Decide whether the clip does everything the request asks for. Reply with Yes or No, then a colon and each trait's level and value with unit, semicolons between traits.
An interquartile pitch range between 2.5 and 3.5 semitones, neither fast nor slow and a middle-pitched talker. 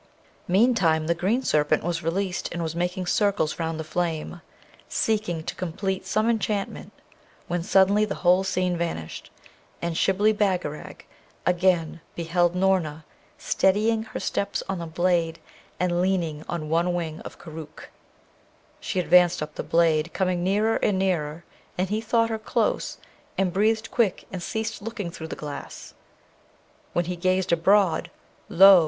Yes: average, 3.0 semitones; average, 150 wpm; medium, 180 Hz